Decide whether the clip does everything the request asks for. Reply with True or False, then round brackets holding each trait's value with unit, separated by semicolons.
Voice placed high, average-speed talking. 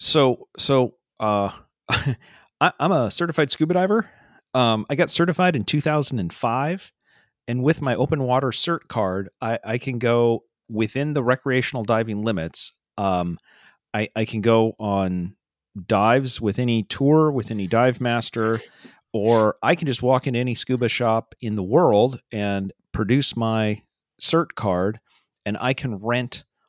False (120 Hz; 155 wpm)